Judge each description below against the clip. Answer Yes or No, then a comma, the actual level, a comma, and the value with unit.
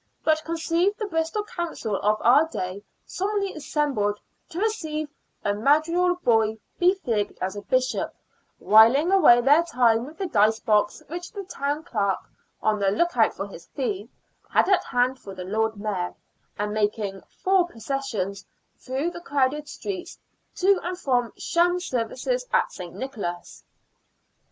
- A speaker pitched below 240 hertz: No, very high, 265 Hz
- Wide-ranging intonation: Yes, wide, 8.4 semitones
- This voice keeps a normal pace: Yes, average, 155 wpm